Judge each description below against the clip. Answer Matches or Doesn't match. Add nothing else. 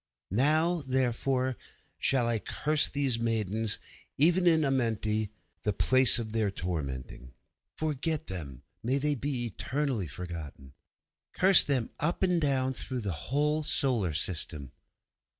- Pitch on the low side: Matches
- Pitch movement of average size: Doesn't match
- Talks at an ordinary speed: Doesn't match